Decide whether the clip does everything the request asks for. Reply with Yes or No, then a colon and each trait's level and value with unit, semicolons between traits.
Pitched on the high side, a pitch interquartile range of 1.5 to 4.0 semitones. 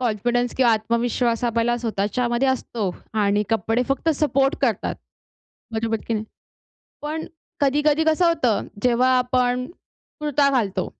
Yes: high, 245 Hz; average, 3.3 semitones